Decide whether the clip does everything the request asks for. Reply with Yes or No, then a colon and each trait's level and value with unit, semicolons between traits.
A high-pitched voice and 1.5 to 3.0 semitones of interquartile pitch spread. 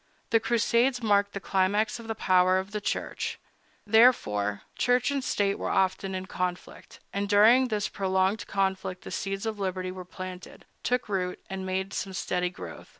Yes: high, 195 Hz; average, 2.7 semitones